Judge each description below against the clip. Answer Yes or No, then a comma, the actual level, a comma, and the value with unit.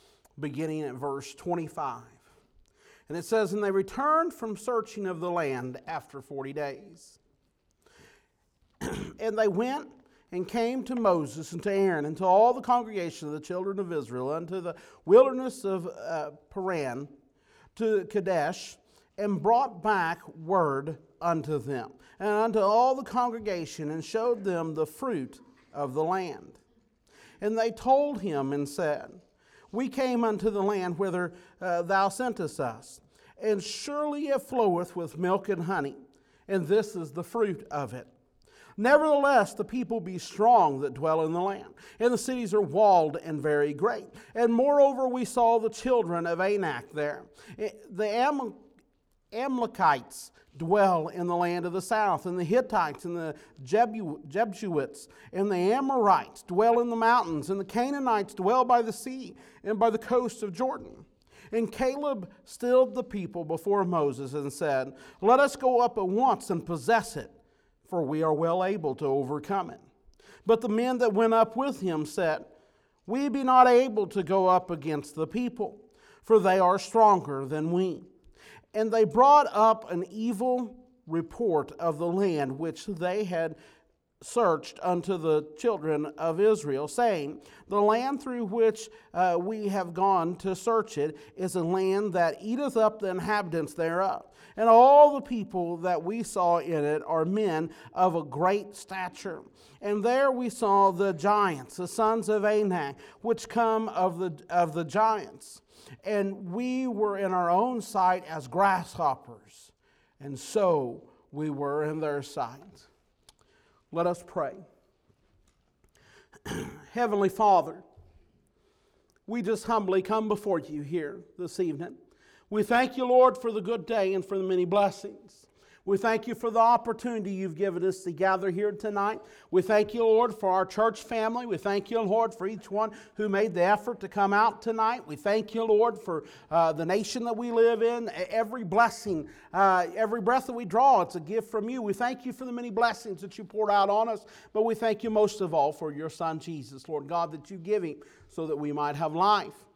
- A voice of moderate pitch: No, high, 200 Hz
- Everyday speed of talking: Yes, average, 170 wpm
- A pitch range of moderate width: Yes, average, 5.0 semitones